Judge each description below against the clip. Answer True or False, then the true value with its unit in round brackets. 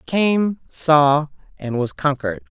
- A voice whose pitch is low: False (150 Hz)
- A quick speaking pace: False (140 wpm)